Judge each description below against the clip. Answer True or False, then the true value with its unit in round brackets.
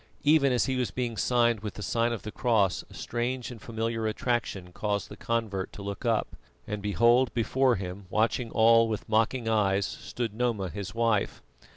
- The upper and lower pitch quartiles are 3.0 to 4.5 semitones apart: False (2.6 semitones)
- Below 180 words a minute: False (185 wpm)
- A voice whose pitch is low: True (115 Hz)